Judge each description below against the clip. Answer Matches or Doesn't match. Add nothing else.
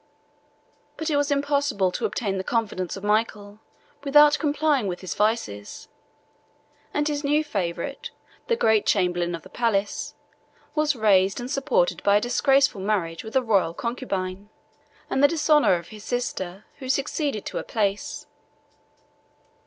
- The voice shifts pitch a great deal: Matches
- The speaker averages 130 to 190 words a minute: Matches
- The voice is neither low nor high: Doesn't match